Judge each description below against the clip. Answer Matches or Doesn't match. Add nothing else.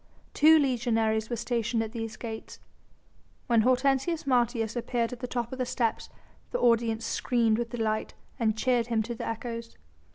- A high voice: Matches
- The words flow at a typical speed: Matches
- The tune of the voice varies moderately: Doesn't match